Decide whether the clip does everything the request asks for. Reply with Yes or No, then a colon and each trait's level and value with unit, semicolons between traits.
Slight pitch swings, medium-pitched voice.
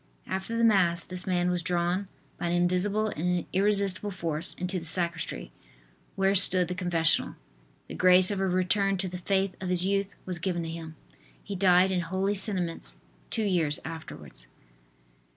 Yes: narrow, 1.9 semitones; medium, 180 Hz